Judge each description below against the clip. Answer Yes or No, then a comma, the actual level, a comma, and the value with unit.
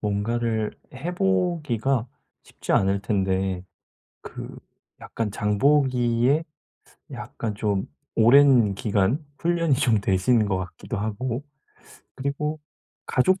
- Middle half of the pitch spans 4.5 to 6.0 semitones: Yes, wide, 5.5 semitones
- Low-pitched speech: Yes, low, 115 Hz